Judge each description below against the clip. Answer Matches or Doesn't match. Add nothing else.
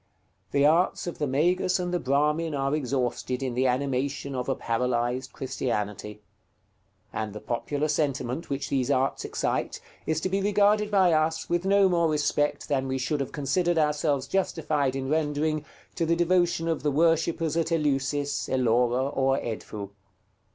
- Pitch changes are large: Doesn't match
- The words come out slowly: Doesn't match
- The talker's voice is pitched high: Doesn't match